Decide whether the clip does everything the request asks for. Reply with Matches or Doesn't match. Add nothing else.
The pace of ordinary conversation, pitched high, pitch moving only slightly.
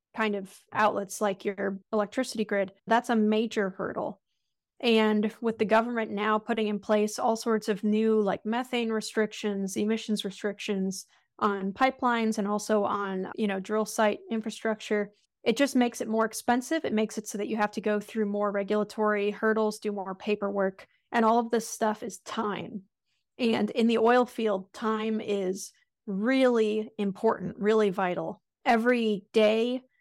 Matches